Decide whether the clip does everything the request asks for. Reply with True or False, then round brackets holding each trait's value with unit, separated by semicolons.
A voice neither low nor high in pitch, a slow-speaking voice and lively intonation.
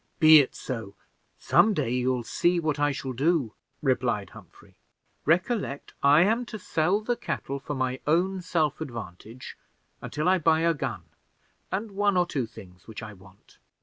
False (145 Hz; 165 wpm; 6.1 semitones)